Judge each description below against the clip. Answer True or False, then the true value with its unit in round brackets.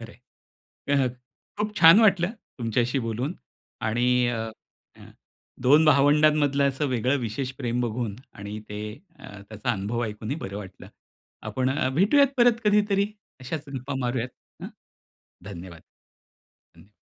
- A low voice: True (130 Hz)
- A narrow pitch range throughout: False (5.4 semitones)